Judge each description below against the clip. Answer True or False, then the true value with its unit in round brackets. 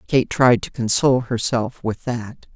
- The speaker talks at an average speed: True (165 wpm)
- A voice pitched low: True (120 Hz)